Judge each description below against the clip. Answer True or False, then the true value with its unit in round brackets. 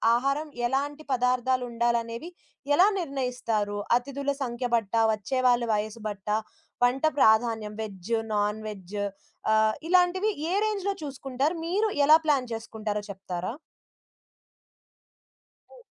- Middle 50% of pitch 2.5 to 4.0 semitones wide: False (4.5 semitones)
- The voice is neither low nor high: False (245 Hz)